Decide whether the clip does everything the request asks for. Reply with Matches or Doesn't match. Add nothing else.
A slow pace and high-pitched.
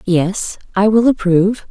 Matches